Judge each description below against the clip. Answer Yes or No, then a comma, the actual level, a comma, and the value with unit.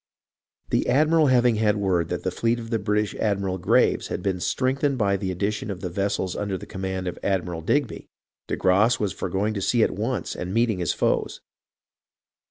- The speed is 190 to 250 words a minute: Yes, average, 200 wpm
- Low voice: Yes, low, 100 Hz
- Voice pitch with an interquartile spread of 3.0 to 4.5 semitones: Yes, average, 3.6 semitones